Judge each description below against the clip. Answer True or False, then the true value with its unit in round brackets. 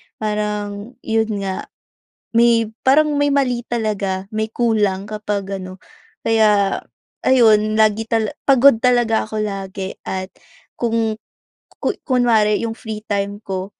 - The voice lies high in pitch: True (215 Hz)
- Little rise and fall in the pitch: True (2.2 semitones)